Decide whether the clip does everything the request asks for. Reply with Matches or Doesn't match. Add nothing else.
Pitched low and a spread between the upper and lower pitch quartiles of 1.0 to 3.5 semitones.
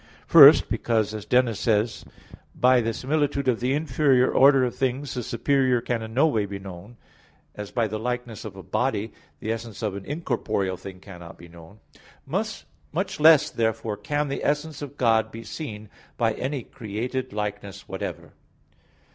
Doesn't match